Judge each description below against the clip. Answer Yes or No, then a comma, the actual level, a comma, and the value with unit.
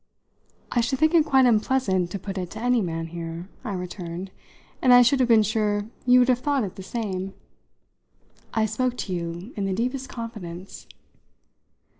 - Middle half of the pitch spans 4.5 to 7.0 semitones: Yes, average, 5.1 semitones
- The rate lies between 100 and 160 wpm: No, average, 180 wpm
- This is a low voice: No, high, 215 Hz